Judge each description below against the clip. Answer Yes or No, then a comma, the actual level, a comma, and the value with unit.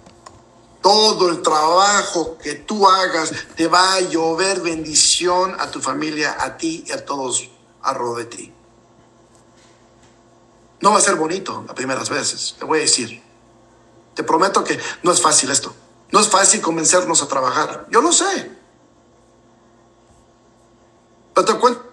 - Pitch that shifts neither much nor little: No, wide, 8.0 semitones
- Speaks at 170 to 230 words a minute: No, average, 150 wpm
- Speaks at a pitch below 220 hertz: Yes, low, 135 Hz